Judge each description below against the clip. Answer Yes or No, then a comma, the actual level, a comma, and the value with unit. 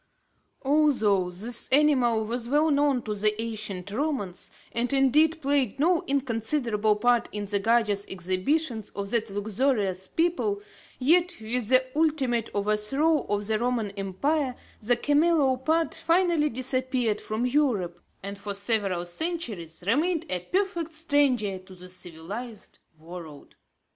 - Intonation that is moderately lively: No, wide, 6.2 semitones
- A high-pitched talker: Yes, high, 235 Hz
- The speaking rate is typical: No, slow, 130 wpm